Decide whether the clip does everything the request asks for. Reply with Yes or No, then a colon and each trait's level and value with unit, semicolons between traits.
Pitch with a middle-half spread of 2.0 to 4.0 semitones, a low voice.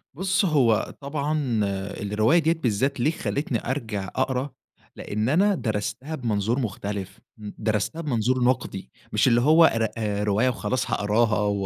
No: average, 5.2 semitones; low, 120 Hz